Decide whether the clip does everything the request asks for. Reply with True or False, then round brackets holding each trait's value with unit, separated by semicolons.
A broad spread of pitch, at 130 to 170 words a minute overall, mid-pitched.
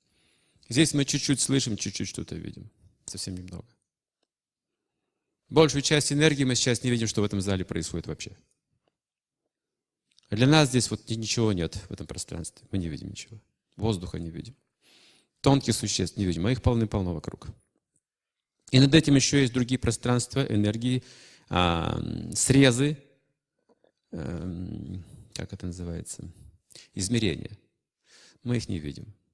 False (5.7 semitones; 135 wpm; 110 Hz)